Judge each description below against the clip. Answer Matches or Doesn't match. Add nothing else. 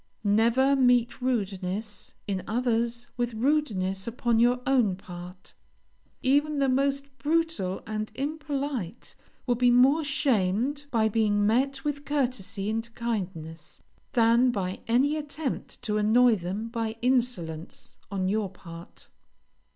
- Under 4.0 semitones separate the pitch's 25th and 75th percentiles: Doesn't match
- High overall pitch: Matches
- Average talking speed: Doesn't match